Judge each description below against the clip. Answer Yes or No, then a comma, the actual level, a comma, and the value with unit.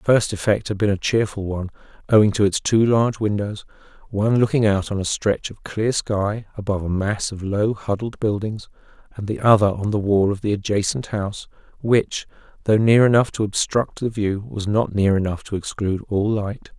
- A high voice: No, low, 105 Hz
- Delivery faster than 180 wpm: Yes, average, 200 wpm